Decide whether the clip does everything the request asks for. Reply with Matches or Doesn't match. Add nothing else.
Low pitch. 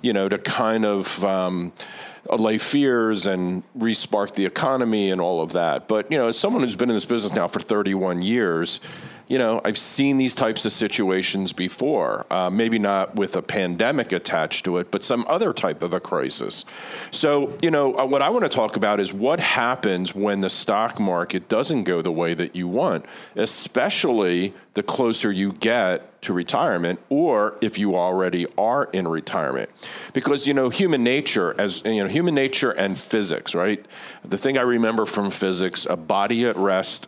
Matches